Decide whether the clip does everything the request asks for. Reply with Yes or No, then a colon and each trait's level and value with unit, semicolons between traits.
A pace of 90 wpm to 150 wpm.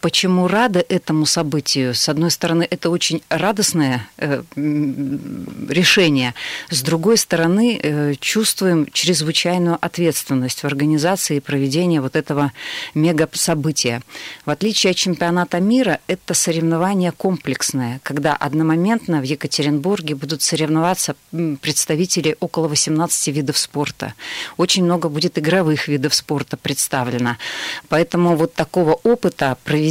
Yes: slow, 110 wpm